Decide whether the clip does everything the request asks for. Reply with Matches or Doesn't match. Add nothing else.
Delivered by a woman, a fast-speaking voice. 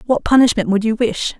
Matches